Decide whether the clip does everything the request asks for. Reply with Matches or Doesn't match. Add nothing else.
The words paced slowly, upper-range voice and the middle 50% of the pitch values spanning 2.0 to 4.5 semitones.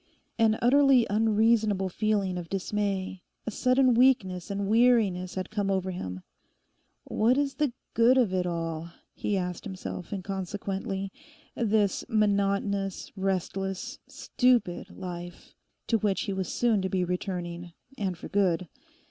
Matches